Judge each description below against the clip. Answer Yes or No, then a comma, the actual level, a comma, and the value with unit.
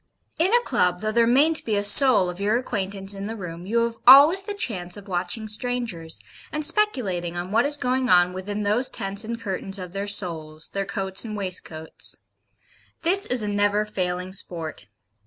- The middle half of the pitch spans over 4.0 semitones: Yes, average, 4.8 semitones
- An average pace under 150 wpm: No, average, 190 wpm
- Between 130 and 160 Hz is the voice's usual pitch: No, high, 205 Hz